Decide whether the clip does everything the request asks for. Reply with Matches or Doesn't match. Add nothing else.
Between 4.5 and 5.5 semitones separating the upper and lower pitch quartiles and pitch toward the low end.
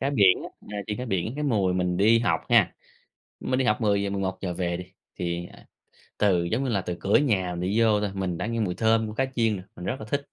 Doesn't match